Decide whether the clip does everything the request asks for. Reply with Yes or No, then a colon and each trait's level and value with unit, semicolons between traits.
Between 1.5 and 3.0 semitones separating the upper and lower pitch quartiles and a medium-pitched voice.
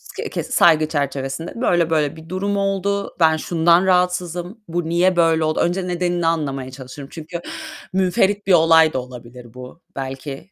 No: average, 3.8 semitones; medium, 165 Hz